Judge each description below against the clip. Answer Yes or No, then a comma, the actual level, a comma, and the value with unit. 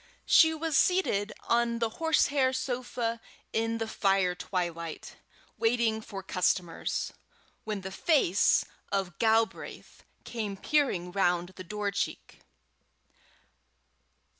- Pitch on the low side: No, high, 220 Hz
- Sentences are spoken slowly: Yes, slow, 105 wpm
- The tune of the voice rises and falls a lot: No, average, 4.0 semitones